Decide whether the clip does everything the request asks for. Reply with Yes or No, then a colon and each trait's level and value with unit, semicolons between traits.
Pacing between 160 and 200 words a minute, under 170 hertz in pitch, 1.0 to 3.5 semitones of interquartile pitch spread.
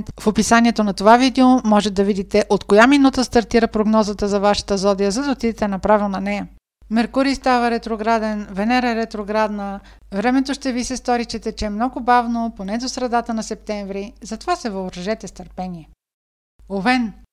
No: fast, 165 wpm; high, 220 Hz; average, 2.9 semitones